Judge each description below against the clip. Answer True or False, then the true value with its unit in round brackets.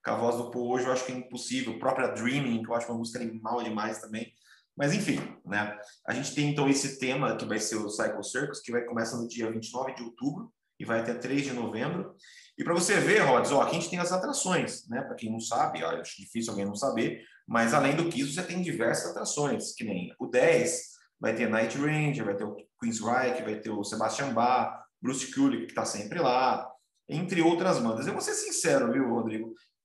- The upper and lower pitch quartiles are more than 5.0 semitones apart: False (4.2 semitones)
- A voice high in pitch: False (125 Hz)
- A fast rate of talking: True (230 wpm)